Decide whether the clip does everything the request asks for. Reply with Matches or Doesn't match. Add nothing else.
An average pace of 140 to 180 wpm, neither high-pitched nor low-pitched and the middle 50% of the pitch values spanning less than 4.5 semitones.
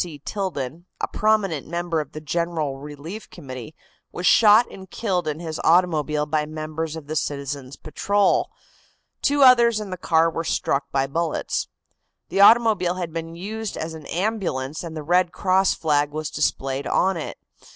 Matches